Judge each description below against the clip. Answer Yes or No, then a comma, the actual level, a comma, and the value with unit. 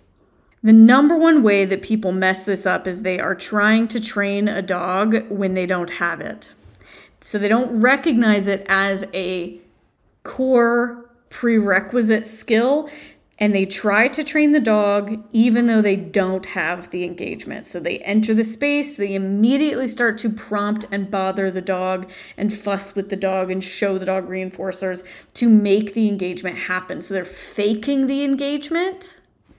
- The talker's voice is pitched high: Yes, high, 205 Hz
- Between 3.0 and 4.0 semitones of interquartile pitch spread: Yes, average, 3.7 semitones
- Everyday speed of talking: Yes, average, 160 wpm